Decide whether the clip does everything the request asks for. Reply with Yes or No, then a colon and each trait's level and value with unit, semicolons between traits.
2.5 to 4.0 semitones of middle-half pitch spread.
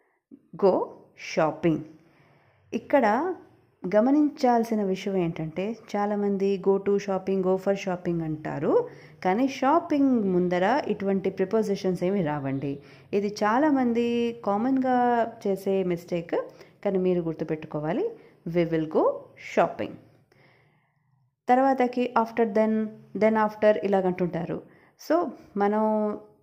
No: average, 5.1 semitones